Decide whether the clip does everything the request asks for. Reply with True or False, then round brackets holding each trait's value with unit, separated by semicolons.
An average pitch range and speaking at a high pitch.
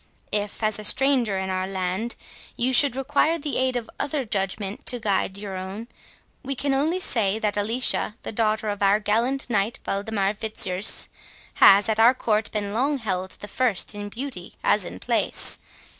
True (4.0 semitones; 215 Hz)